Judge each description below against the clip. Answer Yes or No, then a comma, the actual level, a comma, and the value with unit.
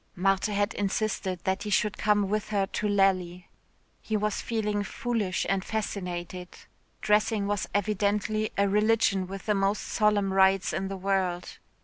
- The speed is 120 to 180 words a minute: Yes, average, 150 wpm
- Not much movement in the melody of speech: Yes, narrow, 1.8 semitones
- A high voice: Yes, high, 200 Hz